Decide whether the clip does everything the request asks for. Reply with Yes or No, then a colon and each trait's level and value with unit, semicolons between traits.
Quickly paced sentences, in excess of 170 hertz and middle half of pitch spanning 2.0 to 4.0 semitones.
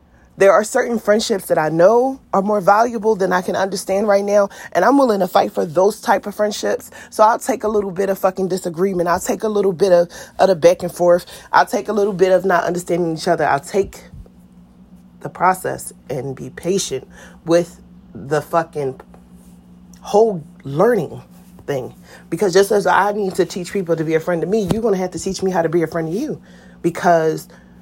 Yes: fast, 210 wpm; medium, 185 Hz; average, 3.6 semitones